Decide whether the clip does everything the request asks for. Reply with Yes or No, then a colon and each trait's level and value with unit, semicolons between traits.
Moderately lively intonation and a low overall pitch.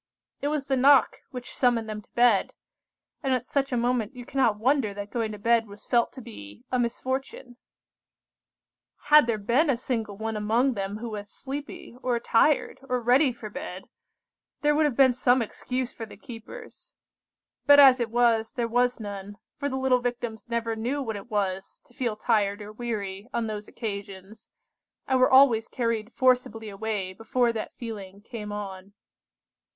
No: average, 3.3 semitones; high, 235 Hz